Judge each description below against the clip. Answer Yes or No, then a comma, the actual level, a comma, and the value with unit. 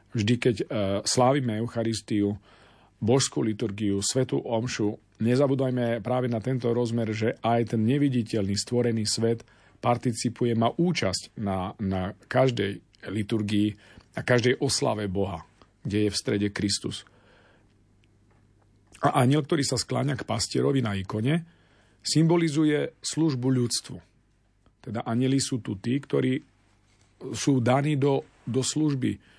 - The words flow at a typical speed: Yes, average, 120 wpm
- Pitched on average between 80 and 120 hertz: Yes, low, 115 Hz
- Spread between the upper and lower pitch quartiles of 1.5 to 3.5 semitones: No, average, 4.0 semitones